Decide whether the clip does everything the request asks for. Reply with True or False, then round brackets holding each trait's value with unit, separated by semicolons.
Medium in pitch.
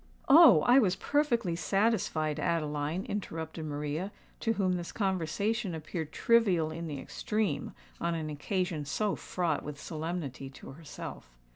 True (170 Hz)